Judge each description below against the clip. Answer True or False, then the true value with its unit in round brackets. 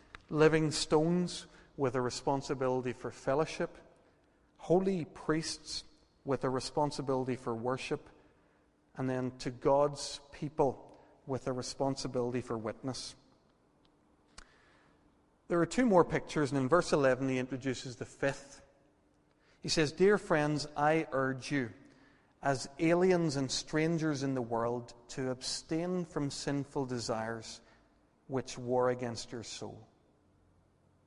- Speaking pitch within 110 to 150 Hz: True (135 Hz)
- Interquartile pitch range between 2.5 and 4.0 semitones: True (3.7 semitones)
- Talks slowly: True (120 wpm)